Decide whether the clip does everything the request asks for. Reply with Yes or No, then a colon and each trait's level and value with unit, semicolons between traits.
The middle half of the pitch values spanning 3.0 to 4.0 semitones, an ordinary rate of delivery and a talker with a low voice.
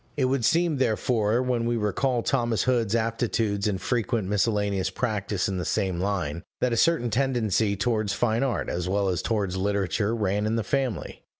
Yes: average, 3.4 semitones; average, 180 wpm; low, 110 Hz